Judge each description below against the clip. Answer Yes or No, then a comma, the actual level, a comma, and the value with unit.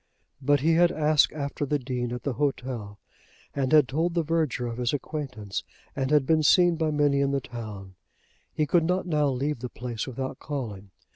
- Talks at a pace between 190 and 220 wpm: Yes, average, 195 wpm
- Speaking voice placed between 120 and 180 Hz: Yes, medium, 140 Hz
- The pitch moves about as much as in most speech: Yes, average, 3.8 semitones